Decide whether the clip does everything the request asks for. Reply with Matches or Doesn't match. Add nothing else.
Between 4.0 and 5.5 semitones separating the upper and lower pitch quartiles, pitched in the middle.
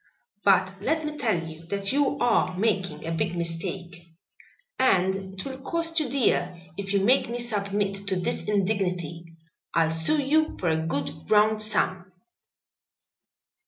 Doesn't match